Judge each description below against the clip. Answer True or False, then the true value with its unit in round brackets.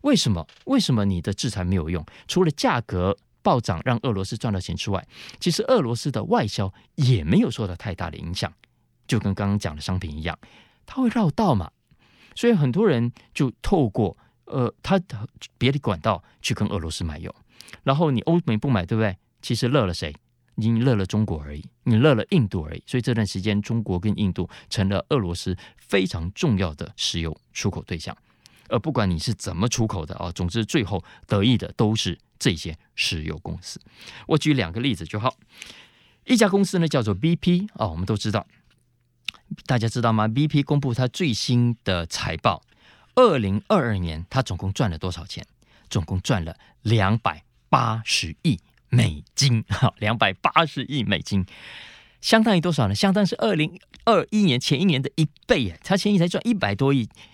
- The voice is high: False (115 Hz)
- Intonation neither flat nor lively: False (5.9 semitones)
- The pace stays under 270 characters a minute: False (280 characters per minute)